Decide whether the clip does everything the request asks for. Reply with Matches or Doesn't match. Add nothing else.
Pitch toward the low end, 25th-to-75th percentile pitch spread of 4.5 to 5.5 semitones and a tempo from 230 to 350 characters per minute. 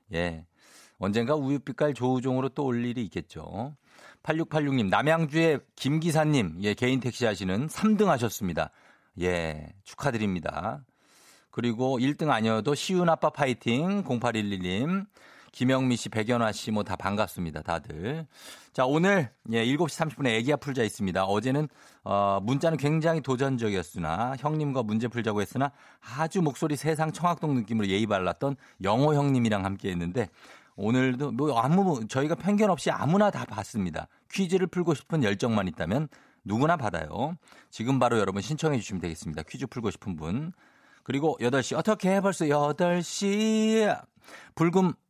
Doesn't match